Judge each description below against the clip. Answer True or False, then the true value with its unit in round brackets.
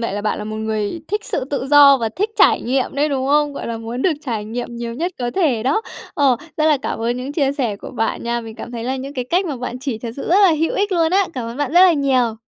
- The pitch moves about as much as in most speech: True (4.3 semitones)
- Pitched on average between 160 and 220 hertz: False (265 Hz)